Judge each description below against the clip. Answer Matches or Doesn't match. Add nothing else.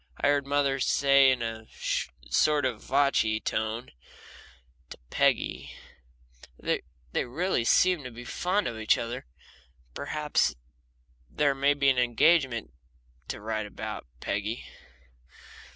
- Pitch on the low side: Matches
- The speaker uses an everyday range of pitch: Matches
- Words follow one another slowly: Matches